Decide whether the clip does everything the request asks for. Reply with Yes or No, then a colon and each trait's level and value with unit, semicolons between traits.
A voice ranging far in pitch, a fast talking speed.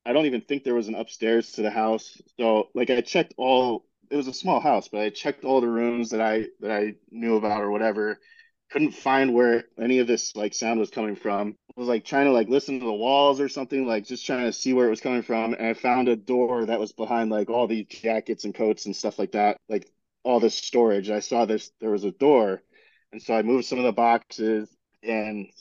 No: narrow, 2.5 semitones; fast, 250 wpm